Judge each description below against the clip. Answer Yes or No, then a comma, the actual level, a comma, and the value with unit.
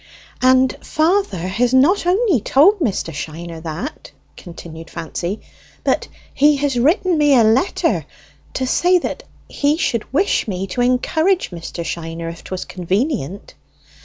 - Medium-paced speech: No, slow, 130 wpm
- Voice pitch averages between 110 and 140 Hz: No, high, 245 Hz